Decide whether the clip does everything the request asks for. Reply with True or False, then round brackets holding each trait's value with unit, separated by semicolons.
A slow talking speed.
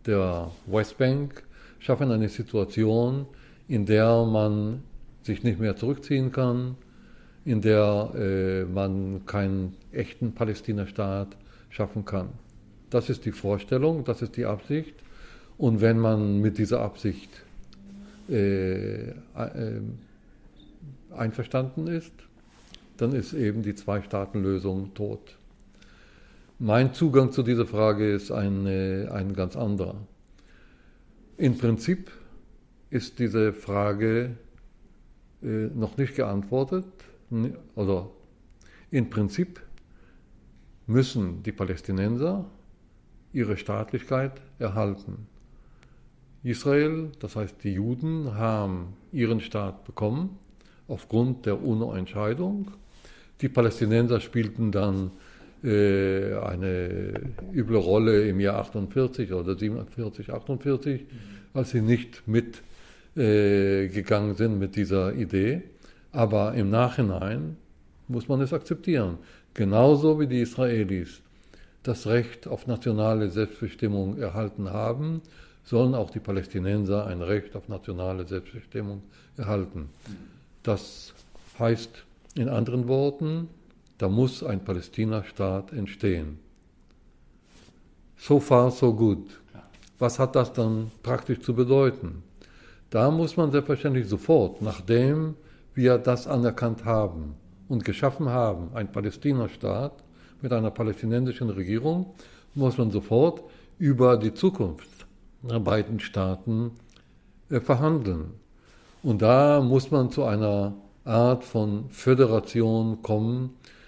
True (105 wpm)